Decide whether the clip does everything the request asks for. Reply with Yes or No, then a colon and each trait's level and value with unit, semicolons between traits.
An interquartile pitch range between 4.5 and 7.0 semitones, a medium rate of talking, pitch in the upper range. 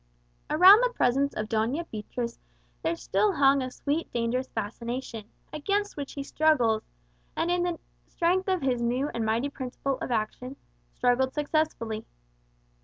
Yes: average, 5.1 semitones; average, 145 wpm; very high, 265 Hz